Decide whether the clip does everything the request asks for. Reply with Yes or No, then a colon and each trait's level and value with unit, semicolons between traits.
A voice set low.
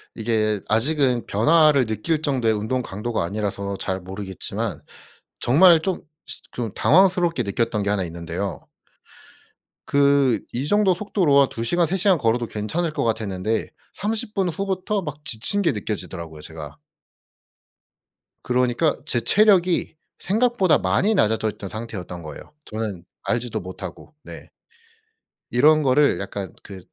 Yes: low, 120 Hz